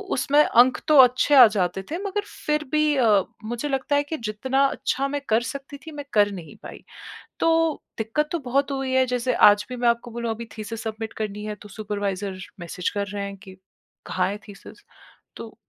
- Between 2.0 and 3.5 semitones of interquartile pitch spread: No, average, 5.0 semitones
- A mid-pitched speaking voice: No, high, 235 Hz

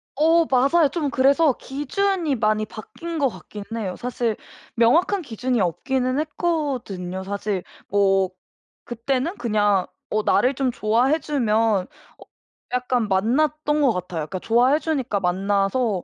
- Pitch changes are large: Yes, wide, 5.8 semitones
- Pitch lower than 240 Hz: No, high, 245 Hz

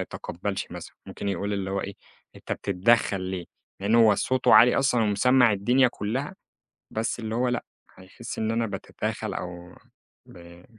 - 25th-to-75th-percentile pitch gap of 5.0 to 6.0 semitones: No, average, 3.8 semitones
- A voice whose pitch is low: Yes, low, 105 Hz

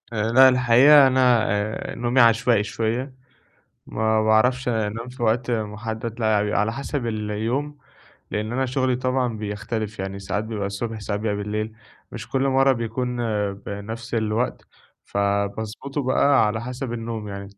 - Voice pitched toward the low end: Yes, low, 115 Hz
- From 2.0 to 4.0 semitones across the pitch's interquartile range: Yes, average, 2.9 semitones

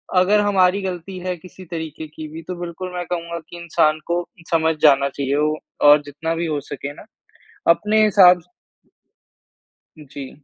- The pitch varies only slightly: No, average, 3.0 semitones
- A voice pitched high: No, medium, 170 Hz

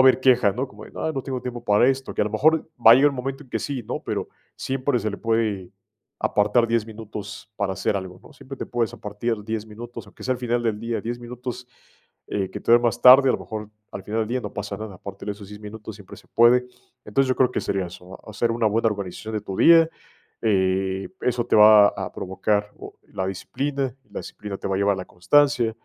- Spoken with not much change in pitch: No, average, 3.4 semitones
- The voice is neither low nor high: No, low, 110 Hz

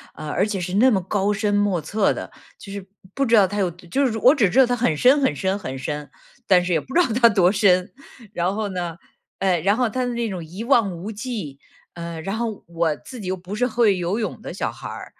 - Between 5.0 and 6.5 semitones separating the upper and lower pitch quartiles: No, average, 4.4 semitones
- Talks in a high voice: Yes, high, 200 Hz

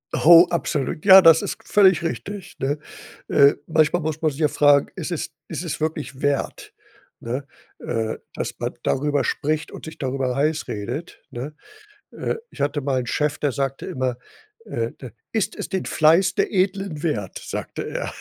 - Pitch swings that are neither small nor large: Yes, average, 3.5 semitones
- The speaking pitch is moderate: Yes, medium, 150 Hz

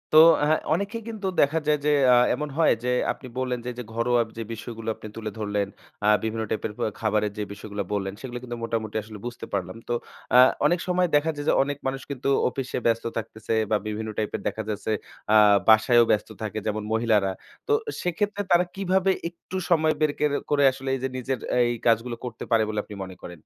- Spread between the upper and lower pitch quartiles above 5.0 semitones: Yes, wide, 5.4 semitones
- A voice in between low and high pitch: No, low, 120 Hz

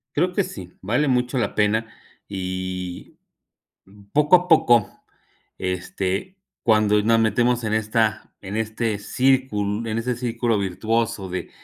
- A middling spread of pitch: Yes, average, 3.3 semitones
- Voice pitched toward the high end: No, low, 110 Hz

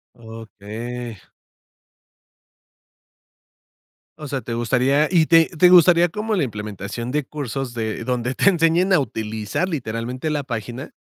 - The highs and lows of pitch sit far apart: Yes, wide, 5.9 semitones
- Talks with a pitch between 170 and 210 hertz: No, low, 130 Hz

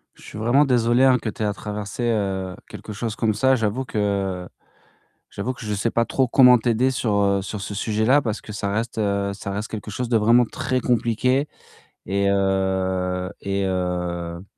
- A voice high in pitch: No, low, 105 Hz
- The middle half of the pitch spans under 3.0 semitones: No, average, 3.3 semitones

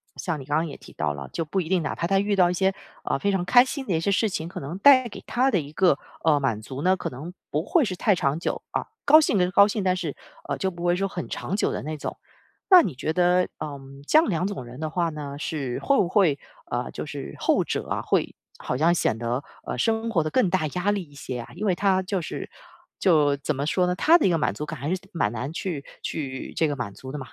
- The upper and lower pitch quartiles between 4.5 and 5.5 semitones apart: Yes, average, 5.0 semitones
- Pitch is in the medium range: Yes, medium, 175 Hz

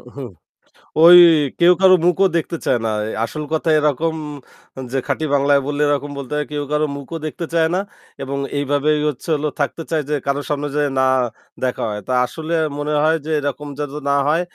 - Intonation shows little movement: Yes, narrow, 2.2 semitones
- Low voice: No, medium, 150 Hz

